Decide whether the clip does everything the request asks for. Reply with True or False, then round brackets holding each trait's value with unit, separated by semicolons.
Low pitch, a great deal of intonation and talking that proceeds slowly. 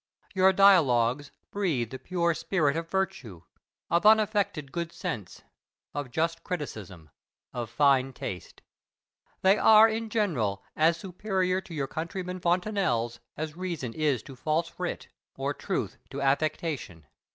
False (165 Hz; 6.1 semitones; 130 wpm)